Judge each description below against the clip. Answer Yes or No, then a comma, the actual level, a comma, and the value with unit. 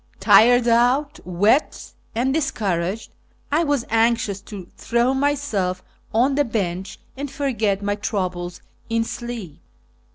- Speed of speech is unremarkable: No, slow, 125 wpm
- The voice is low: No, high, 225 Hz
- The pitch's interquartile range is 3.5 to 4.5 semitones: No, average, 4.9 semitones